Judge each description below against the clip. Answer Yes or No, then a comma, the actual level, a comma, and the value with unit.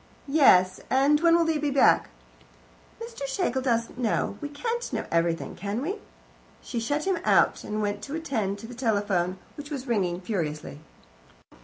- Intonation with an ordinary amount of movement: No, wide, 6.6 semitones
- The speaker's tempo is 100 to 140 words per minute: No, average, 165 wpm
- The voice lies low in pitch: No, high, 240 Hz